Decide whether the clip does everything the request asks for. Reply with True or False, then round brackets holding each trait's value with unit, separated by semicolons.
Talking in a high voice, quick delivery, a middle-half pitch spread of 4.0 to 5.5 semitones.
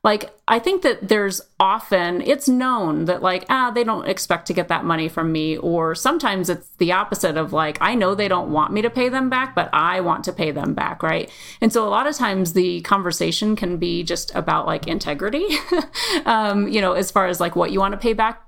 True (195 Hz; 235 wpm; 5.0 semitones)